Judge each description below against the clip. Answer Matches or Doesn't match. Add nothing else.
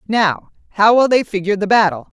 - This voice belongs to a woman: Matches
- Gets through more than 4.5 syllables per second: Matches